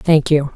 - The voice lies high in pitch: No, medium, 150 Hz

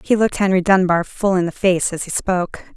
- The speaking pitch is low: No, medium, 185 Hz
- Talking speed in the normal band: No, fast, 240 wpm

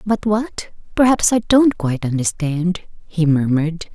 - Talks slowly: Yes, slow, 120 wpm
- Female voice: Yes, female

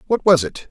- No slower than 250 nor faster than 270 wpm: Yes, fast, 255 wpm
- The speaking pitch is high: No, medium, 160 Hz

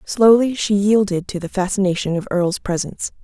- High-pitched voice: Yes, high, 195 Hz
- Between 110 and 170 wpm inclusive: Yes, average, 165 wpm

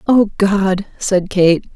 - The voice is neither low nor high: No, high, 195 Hz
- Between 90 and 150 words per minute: Yes, slow, 135 wpm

